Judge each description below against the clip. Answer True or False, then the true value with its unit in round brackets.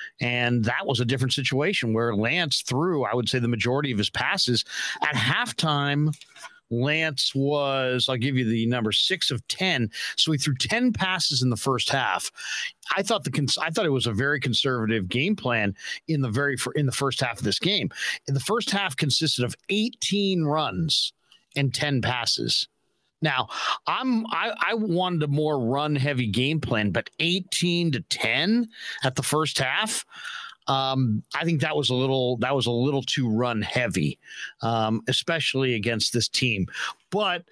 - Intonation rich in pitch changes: False (4.4 semitones)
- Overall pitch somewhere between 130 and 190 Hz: True (135 Hz)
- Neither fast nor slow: True (180 wpm)